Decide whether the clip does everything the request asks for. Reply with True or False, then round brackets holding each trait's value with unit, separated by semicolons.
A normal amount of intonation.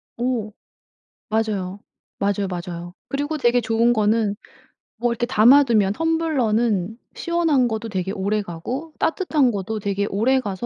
True (4.3 semitones)